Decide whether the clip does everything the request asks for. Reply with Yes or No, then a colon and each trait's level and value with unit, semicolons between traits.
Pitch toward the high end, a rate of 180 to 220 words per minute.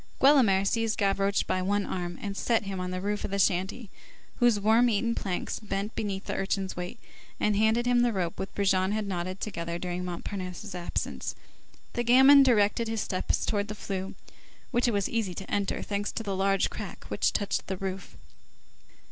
Yes: high, 200 Hz; average, 185 wpm